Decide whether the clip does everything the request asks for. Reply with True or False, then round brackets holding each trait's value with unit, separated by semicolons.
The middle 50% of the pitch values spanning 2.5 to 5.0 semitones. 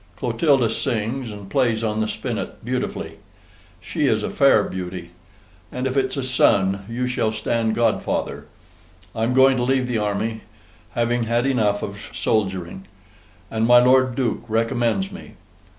True (3.0 semitones)